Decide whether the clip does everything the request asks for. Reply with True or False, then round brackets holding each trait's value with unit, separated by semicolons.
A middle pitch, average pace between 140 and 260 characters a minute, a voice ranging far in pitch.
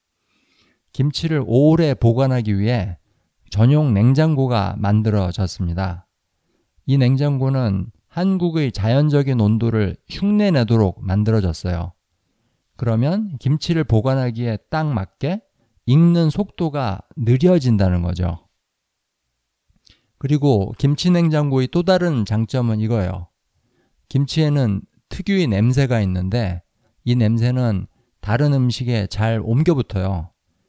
False (120 Hz; 240 characters per minute; 6.5 semitones)